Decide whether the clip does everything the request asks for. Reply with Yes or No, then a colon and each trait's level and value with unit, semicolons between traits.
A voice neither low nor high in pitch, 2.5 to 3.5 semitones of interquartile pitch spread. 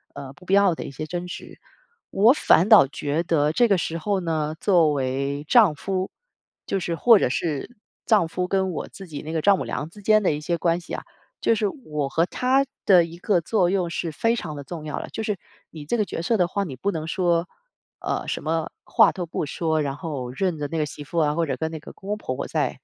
No: medium, 170 Hz; average, 4.3 semitones